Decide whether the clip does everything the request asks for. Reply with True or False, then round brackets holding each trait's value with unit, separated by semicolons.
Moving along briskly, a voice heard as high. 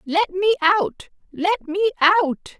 False (140 wpm; 365 Hz)